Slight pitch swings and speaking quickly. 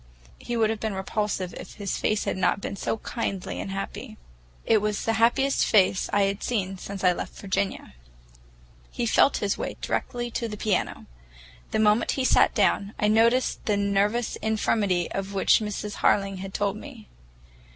No: narrow, 2.2 semitones; average, 175 wpm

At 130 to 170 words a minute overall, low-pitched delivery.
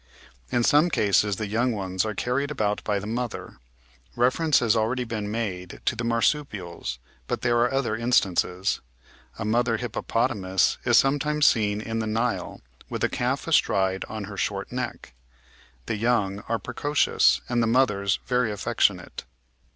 Yes: average, 155 wpm; low, 115 Hz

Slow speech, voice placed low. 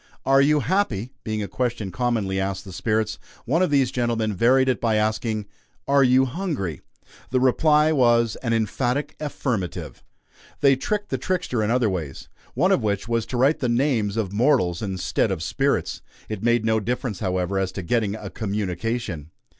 No: average, 175 wpm; low, 115 Hz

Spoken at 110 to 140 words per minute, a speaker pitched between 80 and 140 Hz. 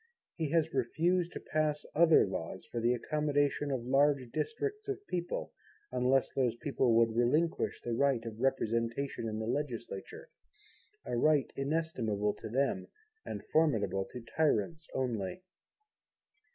Yes: slow, 135 wpm; low, 135 Hz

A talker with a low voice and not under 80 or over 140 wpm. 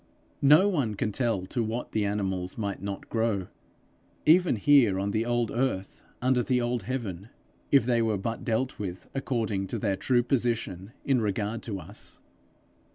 No: low, 115 Hz; average, 165 wpm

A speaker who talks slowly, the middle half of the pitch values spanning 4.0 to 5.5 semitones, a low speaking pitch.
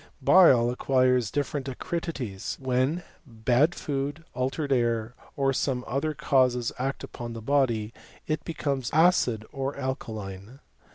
No: slow, 125 wpm; average, 3.0 semitones; low, 130 Hz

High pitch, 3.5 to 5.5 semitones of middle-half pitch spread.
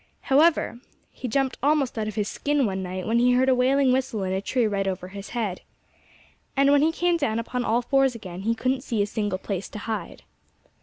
Yes: high, 235 Hz; average, 4.8 semitones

